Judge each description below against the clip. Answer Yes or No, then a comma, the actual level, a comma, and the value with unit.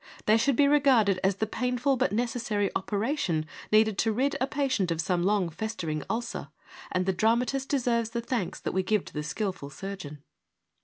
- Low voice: No, high, 215 Hz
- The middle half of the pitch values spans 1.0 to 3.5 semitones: No, average, 4.8 semitones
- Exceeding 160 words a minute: Yes, average, 185 wpm